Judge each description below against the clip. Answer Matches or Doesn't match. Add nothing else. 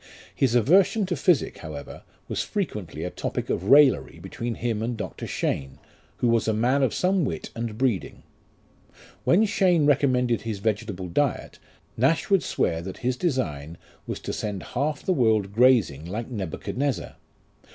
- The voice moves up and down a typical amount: Doesn't match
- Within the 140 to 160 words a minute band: Matches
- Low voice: Matches